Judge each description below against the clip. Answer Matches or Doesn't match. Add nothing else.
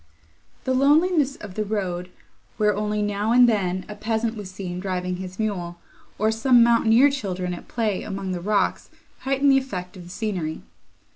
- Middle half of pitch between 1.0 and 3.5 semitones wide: Doesn't match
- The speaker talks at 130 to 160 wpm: Doesn't match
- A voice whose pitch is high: Matches